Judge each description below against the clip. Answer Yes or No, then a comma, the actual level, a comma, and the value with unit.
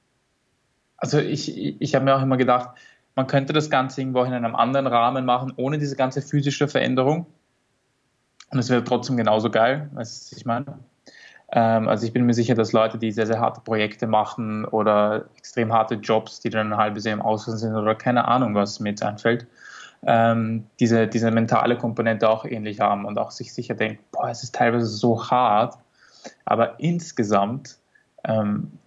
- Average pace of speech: Yes, average, 180 wpm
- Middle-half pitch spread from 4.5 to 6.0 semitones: No, average, 2.8 semitones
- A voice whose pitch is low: Yes, low, 120 Hz